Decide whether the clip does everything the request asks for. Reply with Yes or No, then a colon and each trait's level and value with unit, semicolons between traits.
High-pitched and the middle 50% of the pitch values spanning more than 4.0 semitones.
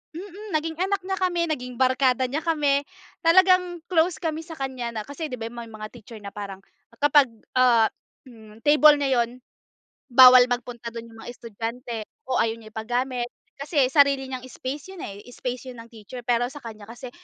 Yes: very high, 255 Hz; average, 4.6 semitones